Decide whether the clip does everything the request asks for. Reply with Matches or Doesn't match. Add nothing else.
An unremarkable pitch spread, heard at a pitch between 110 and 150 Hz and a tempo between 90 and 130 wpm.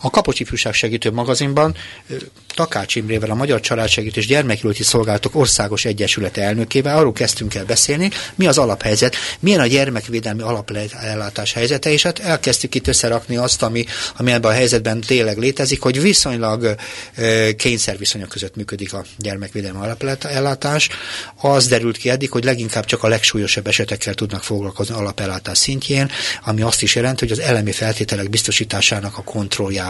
Doesn't match